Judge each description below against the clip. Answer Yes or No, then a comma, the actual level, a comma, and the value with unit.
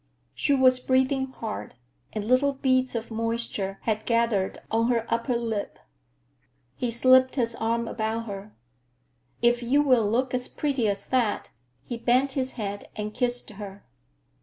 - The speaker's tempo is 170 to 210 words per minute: No, average, 150 wpm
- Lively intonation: No, average, 2.8 semitones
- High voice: Yes, high, 235 Hz